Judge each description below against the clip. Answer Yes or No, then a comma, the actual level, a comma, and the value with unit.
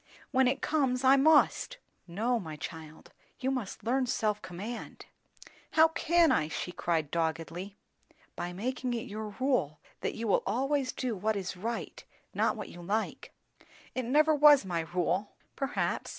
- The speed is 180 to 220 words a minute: No, average, 155 wpm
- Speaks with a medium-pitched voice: No, high, 225 Hz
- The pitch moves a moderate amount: No, wide, 6.9 semitones